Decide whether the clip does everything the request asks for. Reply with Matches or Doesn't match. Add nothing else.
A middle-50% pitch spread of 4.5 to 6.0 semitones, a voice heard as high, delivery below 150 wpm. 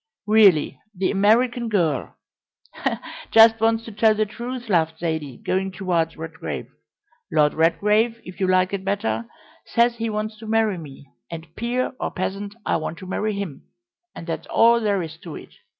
Doesn't match